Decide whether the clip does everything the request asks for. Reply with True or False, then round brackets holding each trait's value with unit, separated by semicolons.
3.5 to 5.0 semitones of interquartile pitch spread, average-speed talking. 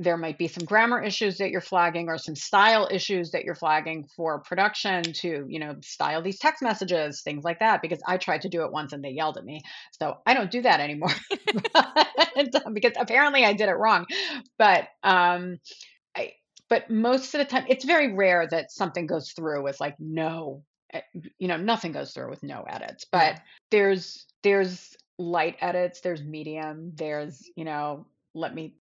False (5.6 semitones; 185 wpm)